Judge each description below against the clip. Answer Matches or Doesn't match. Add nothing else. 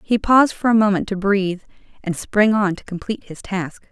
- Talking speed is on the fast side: Matches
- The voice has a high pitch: Matches